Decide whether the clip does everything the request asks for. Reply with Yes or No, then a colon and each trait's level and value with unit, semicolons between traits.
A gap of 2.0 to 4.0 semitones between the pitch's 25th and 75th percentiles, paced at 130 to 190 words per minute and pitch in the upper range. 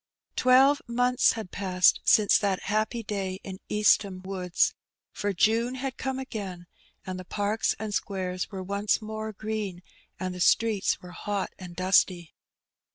Yes: average, 2.9 semitones; average, 155 wpm; high, 200 Hz